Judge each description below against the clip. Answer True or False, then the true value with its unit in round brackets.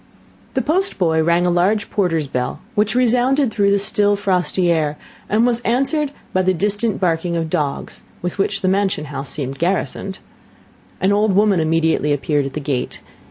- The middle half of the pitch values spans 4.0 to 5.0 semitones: True (4.5 semitones)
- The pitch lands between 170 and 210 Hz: True (185 Hz)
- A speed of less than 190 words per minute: True (175 wpm)